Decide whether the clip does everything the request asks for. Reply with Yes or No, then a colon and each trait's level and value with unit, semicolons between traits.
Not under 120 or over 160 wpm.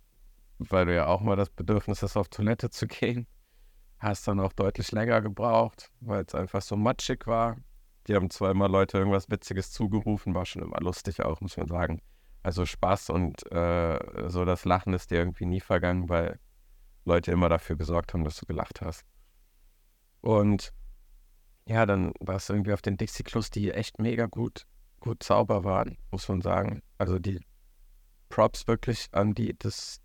No: average, 175 wpm